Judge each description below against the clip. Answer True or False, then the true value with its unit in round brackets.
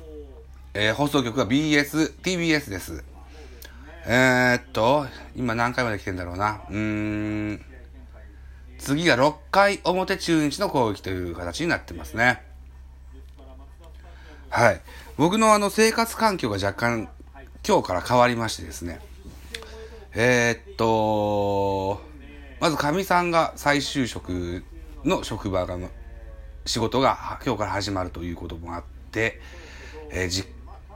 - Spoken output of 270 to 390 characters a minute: False (200 characters per minute)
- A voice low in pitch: True (90 Hz)